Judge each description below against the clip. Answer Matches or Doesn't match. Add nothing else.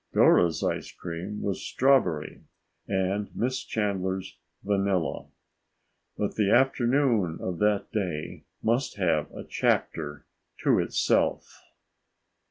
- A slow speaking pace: Matches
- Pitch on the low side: Matches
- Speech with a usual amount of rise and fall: Matches